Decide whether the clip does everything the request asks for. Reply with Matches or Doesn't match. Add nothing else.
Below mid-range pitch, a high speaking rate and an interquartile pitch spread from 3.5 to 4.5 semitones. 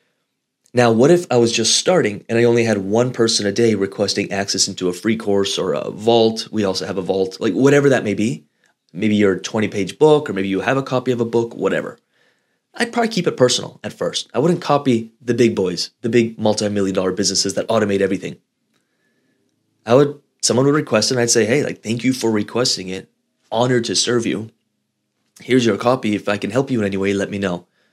Matches